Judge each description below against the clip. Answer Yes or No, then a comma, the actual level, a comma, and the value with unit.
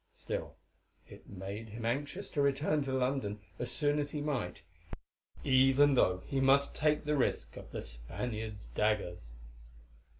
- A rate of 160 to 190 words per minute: No, average, 145 wpm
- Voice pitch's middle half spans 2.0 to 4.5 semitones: No, wide, 5.5 semitones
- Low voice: Yes, low, 130 Hz